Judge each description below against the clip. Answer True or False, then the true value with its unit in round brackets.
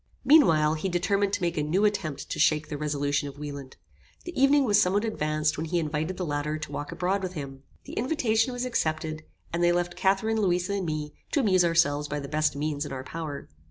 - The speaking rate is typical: False (220 wpm)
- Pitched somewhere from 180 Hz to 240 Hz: False (165 Hz)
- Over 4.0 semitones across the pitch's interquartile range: True (4.8 semitones)